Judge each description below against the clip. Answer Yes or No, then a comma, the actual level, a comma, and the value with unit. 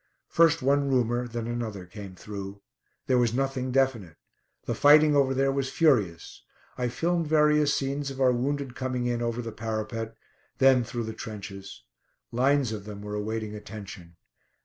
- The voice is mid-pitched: No, low, 120 Hz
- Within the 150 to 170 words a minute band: Yes, average, 160 wpm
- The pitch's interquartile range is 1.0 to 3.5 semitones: No, average, 4.1 semitones